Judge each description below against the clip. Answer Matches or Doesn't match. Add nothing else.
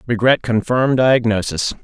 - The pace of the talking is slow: Matches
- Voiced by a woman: Doesn't match